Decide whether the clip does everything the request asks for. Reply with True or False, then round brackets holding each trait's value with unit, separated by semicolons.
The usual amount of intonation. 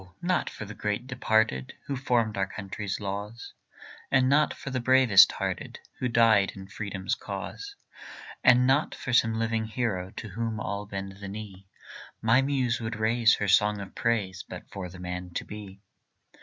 True (3.6 semitones)